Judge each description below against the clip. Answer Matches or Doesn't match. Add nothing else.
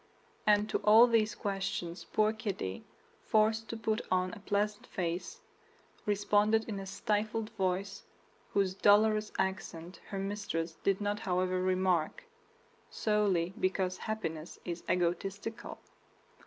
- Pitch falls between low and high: Doesn't match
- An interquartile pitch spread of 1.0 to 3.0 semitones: Matches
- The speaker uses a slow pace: Matches